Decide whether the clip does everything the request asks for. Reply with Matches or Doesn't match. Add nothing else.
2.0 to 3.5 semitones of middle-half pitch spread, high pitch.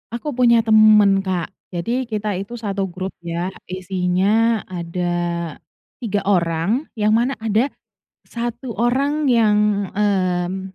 Doesn't match